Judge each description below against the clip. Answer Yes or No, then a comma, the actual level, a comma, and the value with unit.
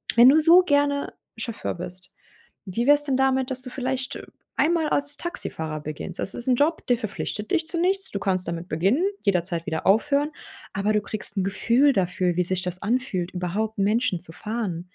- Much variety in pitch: Yes, wide, 7.2 semitones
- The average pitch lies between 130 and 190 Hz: No, high, 220 Hz